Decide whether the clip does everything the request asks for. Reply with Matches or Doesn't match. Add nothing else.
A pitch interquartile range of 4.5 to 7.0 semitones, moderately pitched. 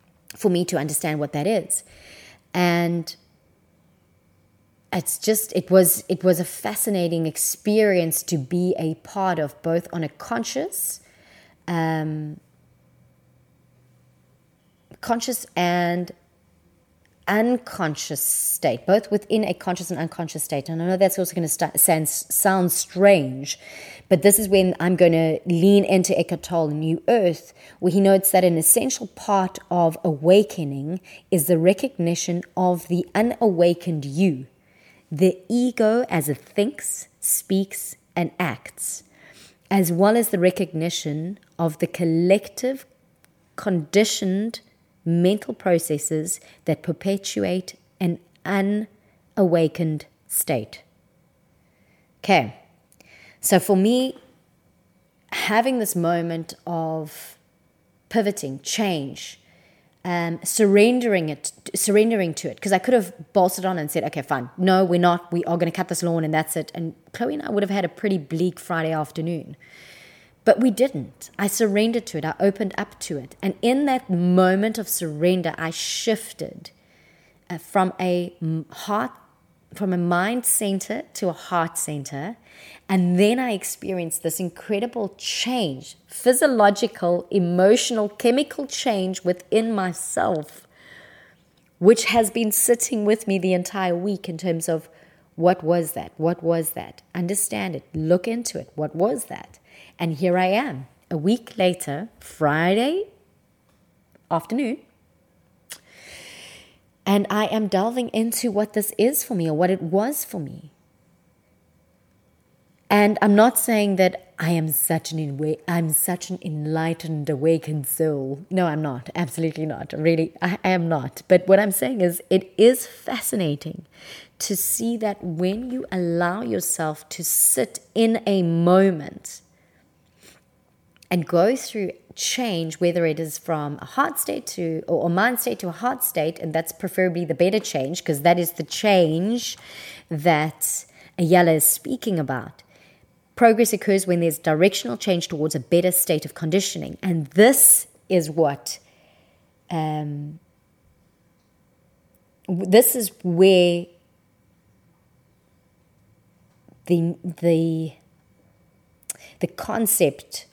Doesn't match